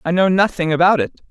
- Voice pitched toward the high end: No, medium, 175 Hz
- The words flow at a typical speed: No, fast, 230 wpm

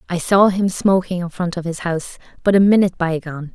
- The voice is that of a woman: Yes, female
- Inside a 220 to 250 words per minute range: Yes, fast, 235 wpm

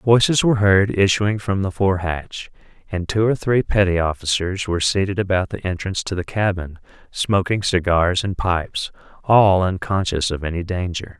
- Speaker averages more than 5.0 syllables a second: No, 4.9 syllables/s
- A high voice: No, very low, 95 Hz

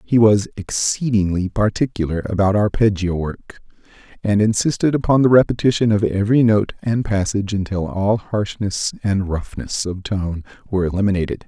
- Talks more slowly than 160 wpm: Yes, slow, 135 wpm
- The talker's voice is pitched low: Yes, low, 105 Hz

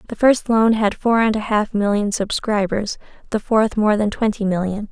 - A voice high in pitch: Yes, high, 210 Hz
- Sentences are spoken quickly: No, average, 195 wpm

